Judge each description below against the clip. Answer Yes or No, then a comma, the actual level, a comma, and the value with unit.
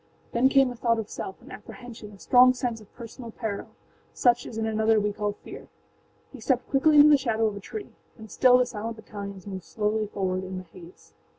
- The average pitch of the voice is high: Yes, high, 220 Hz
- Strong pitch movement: No, average, 3.4 semitones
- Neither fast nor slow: No, fast, 210 wpm